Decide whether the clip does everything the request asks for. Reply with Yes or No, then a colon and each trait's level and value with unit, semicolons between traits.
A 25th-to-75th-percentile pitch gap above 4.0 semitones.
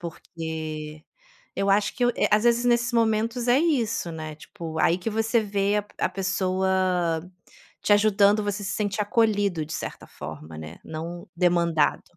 Yes: average, 4.5 semitones